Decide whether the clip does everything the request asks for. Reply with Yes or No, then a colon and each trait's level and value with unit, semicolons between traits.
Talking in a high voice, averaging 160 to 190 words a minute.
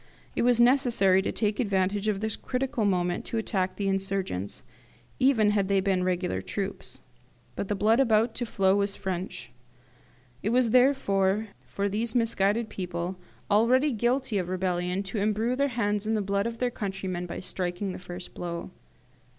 Yes: high, 200 Hz; average, 165 wpm